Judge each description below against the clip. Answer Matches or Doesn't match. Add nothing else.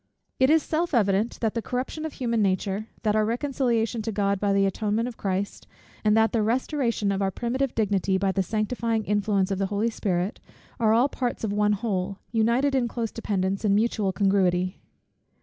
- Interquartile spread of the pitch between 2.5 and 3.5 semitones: Matches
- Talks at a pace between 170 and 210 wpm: Matches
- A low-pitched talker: Doesn't match